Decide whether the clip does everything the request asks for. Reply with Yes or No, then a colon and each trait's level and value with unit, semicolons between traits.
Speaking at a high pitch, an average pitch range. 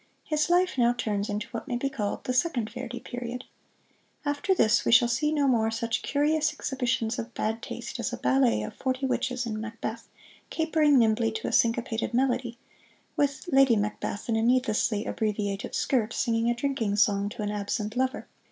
Yes: high, 235 Hz; average, 3.2 semitones